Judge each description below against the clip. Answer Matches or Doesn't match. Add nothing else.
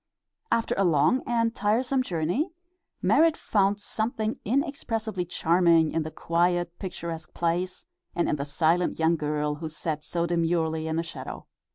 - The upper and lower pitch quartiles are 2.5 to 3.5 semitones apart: Doesn't match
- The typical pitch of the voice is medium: Matches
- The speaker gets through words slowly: Doesn't match